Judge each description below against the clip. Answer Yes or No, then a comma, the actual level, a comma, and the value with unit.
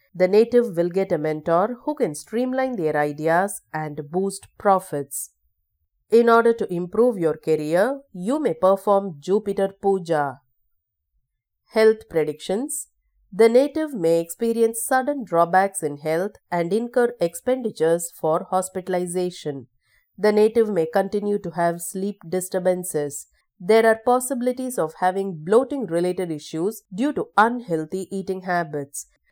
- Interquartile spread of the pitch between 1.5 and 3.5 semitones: No, wide, 5.6 semitones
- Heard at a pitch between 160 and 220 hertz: Yes, medium, 185 Hz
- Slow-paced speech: Yes, slow, 125 wpm